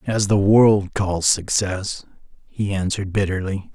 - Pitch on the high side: No, very low, 95 Hz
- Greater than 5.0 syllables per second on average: No, 4.0 syllables/s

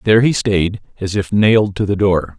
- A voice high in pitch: No, low, 100 Hz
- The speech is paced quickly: Yes, fast, 225 wpm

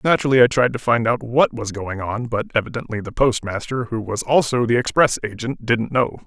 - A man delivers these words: Yes, male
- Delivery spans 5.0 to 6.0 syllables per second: Yes, 5.6 syllables/s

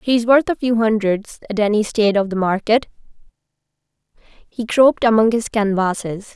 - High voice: Yes, high, 220 Hz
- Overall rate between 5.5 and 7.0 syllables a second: No, 5.1 syllables/s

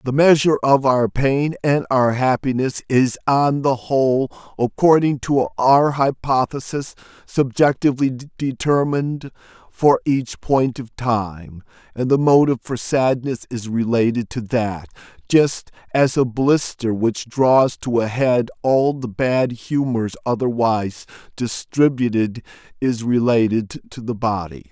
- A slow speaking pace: Yes, slow, 125 wpm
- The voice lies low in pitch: Yes, low, 125 Hz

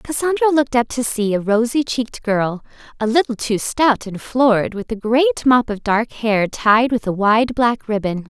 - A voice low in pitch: No, high, 235 Hz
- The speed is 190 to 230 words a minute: Yes, average, 200 wpm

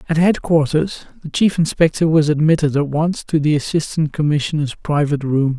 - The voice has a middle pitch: Yes, medium, 155 Hz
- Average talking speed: Yes, average, 160 wpm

